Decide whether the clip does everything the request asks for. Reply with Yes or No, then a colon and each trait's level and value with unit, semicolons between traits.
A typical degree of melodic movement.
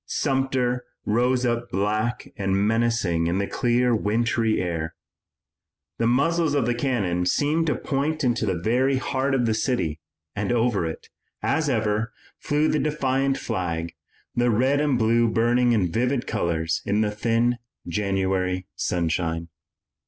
Yes: average, 5.0 semitones